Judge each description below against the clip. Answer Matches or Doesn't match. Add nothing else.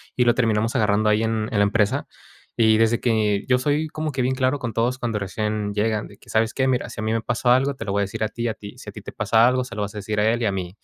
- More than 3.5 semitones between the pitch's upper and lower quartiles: Doesn't match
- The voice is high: Doesn't match